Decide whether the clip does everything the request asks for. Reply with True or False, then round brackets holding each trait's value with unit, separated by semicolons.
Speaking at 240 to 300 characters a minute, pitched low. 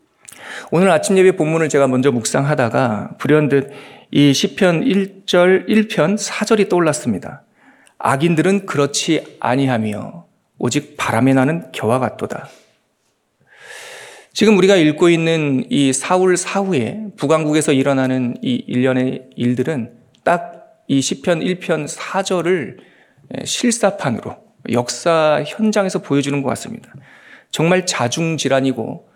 False (250 characters per minute; 160 Hz)